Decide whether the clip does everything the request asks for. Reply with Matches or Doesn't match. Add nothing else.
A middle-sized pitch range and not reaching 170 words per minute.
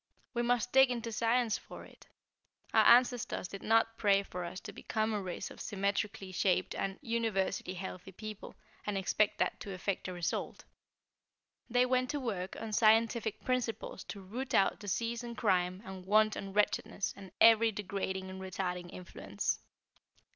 Matches